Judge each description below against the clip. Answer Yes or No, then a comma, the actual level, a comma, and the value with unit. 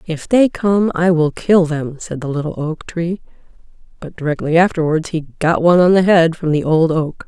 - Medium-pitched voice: Yes, medium, 165 Hz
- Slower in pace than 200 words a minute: No, fast, 205 wpm